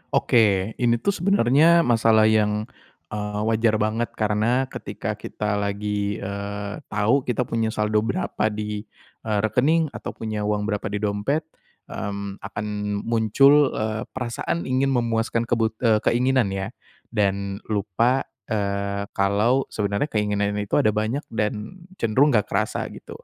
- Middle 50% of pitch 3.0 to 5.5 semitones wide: No, narrow, 2.5 semitones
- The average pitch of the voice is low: Yes, low, 110 Hz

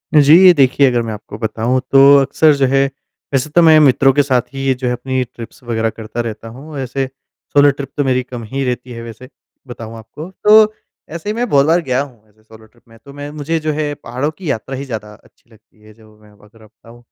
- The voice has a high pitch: No, low, 130 Hz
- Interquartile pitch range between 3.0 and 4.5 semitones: Yes, average, 4.1 semitones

